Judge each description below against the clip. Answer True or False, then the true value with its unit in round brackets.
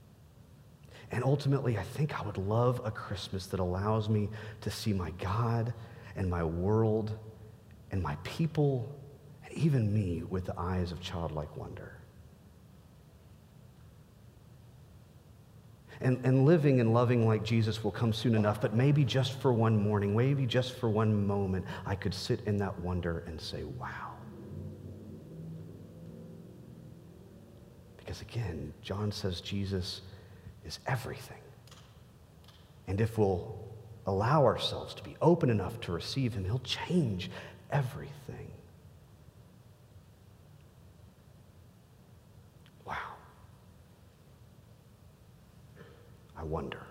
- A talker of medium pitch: False (110 Hz)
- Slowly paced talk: True (110 wpm)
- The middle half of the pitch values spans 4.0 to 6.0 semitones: True (4.4 semitones)